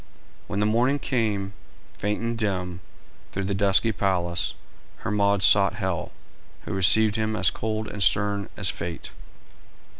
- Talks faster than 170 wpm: No, average, 140 wpm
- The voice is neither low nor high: No, low, 100 Hz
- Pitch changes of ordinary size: No, narrow, 2.1 semitones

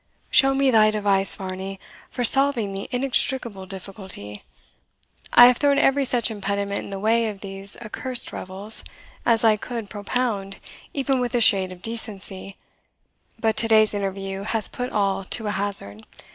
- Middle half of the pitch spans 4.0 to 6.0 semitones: No, average, 3.6 semitones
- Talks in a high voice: Yes, high, 210 Hz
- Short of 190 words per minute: Yes, average, 160 wpm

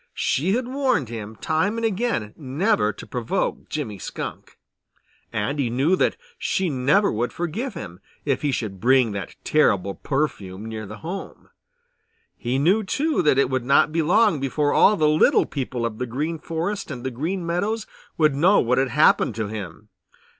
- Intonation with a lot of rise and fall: Yes, wide, 7.7 semitones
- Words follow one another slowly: No, average, 175 wpm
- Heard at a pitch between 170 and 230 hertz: No, medium, 140 Hz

